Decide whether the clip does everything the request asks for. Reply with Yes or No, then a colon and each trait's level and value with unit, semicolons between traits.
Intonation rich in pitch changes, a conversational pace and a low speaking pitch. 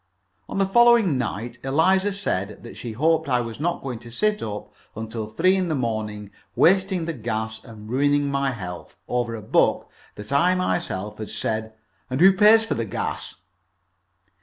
Yes: wide, 8.7 semitones; average, 175 wpm; low, 130 Hz